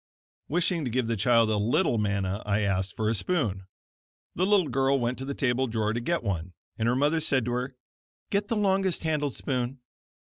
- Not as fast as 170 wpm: No, average, 200 wpm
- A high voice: No, low, 125 Hz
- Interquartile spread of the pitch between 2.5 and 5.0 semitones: No, wide, 5.4 semitones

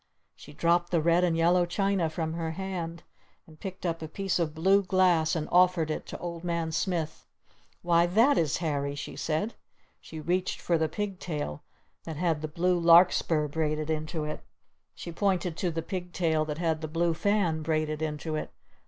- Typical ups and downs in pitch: No, narrow, 2.3 semitones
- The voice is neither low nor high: Yes, medium, 165 Hz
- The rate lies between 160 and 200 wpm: Yes, average, 190 wpm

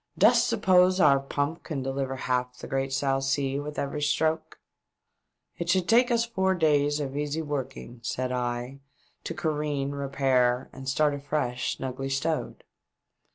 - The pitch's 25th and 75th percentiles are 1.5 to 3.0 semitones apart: Yes, narrow, 2.5 semitones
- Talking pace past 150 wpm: Yes, average, 160 wpm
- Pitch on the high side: No, medium, 140 Hz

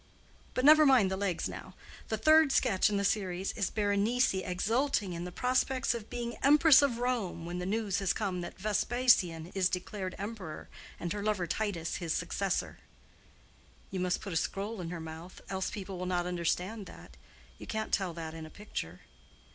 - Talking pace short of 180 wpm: No, average, 185 wpm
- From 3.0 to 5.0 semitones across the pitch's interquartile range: Yes, average, 4.1 semitones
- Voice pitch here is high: Yes, high, 195 Hz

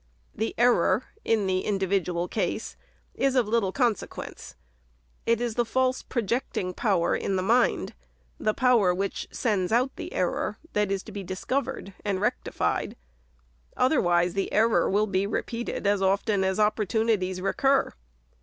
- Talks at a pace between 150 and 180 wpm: Yes, average, 160 wpm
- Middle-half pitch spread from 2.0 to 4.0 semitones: Yes, average, 3.7 semitones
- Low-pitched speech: No, high, 210 Hz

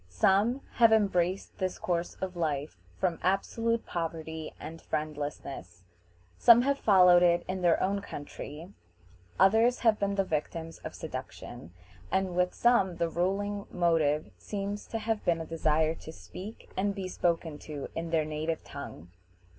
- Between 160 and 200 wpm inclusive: No, average, 150 wpm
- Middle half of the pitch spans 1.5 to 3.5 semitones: No, average, 3.9 semitones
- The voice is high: No, medium, 175 Hz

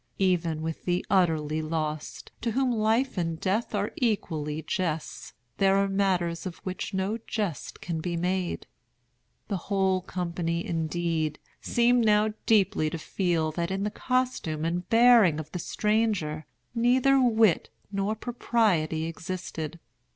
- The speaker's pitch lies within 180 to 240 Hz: Yes, medium, 185 Hz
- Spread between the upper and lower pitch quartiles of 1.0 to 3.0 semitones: No, average, 4.7 semitones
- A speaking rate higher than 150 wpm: No, slow, 135 wpm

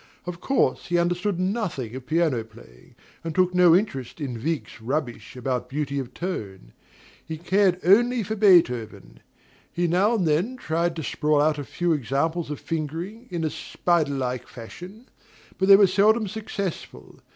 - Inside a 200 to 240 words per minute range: No, average, 165 wpm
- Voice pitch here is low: No, medium, 165 Hz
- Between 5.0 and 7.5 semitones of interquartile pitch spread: Yes, wide, 5.5 semitones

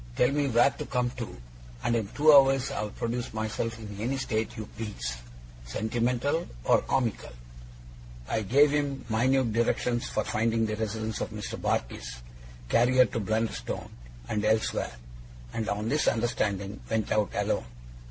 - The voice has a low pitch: Yes, low, 115 Hz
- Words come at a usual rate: Yes, average, 150 wpm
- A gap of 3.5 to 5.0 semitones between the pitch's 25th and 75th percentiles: No, average, 2.7 semitones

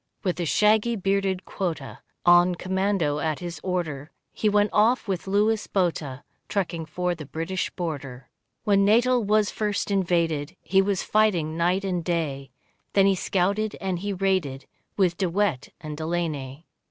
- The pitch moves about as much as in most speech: Yes, average, 3.8 semitones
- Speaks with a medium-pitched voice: Yes, medium, 180 Hz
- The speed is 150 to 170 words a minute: Yes, average, 155 wpm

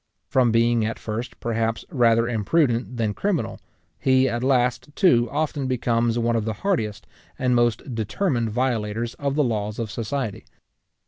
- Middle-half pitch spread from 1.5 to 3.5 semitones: Yes, narrow, 2.5 semitones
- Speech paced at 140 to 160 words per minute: Yes, average, 150 wpm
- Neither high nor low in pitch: No, low, 120 Hz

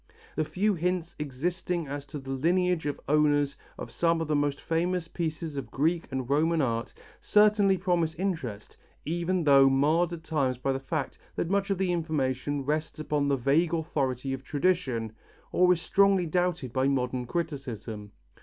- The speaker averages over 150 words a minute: Yes, average, 170 wpm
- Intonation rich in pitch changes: No, average, 4.3 semitones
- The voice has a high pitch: No, medium, 155 Hz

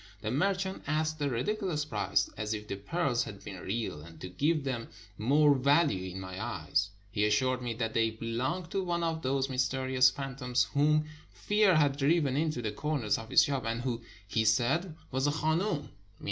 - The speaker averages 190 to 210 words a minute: Yes, average, 195 wpm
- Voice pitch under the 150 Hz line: Yes, low, 135 Hz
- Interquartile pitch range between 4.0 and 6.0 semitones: Yes, average, 5.3 semitones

